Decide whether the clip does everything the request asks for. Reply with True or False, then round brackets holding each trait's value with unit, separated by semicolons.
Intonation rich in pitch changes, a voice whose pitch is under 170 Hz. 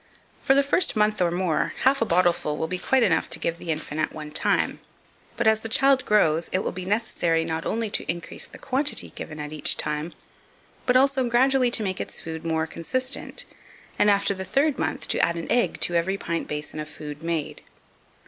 False (6.8 semitones; 180 Hz)